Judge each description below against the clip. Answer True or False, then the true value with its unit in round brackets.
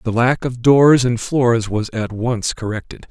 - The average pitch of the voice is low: True (120 Hz)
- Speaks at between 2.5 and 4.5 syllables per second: True (4.0 syllables/s)